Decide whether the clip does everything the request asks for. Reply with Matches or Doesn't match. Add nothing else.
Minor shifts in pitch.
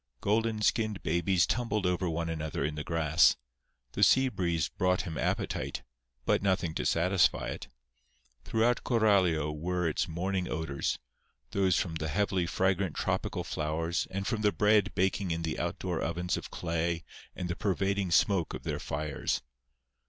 Doesn't match